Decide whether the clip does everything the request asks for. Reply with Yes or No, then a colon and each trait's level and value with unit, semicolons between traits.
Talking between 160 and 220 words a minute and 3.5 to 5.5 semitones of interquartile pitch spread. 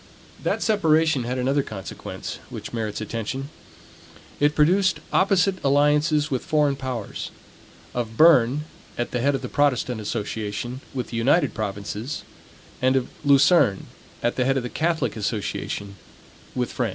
No: average, 140 wpm; average, 4.4 semitones